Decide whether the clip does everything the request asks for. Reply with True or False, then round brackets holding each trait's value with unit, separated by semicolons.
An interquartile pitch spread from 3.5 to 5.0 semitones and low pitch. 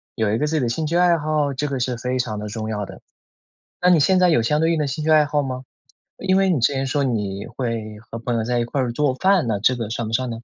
True (4.7 semitones; 130 Hz)